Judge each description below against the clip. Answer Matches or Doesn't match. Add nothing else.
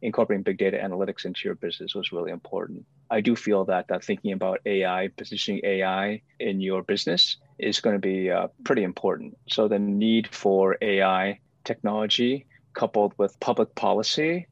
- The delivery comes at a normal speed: Matches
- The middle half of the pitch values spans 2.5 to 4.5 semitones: Matches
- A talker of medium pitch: Doesn't match